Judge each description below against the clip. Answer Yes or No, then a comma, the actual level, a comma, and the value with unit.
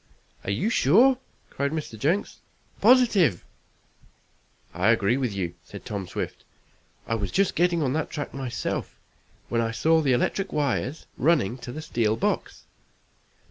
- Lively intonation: Yes, wide, 6.3 semitones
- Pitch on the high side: No, low, 135 Hz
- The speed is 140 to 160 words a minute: Yes, average, 145 wpm